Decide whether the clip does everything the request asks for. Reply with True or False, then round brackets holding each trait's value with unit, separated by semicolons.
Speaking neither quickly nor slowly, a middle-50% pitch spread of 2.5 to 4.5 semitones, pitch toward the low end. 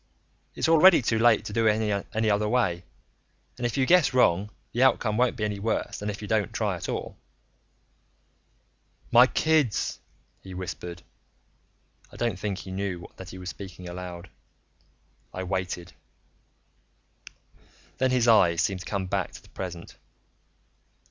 True (155 wpm; 4.2 semitones; 105 Hz)